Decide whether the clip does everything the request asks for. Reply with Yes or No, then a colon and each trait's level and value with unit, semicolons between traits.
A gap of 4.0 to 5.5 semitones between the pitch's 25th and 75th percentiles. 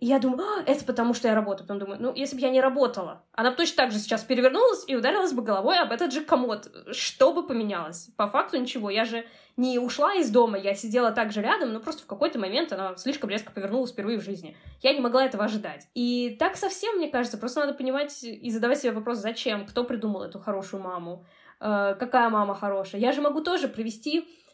Yes: average, 4.5 semitones